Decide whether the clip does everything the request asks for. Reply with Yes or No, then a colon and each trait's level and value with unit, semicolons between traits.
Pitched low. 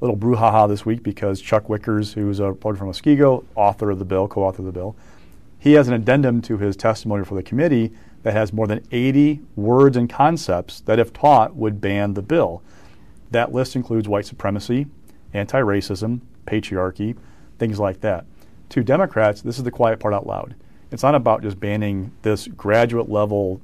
Yes: low, 110 Hz